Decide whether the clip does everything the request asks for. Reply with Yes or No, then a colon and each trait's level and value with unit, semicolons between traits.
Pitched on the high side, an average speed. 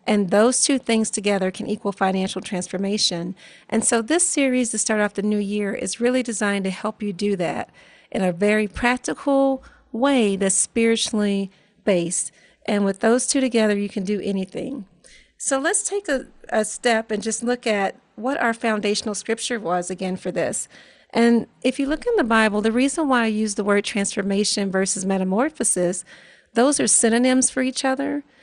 Yes: high, 215 Hz; average, 180 wpm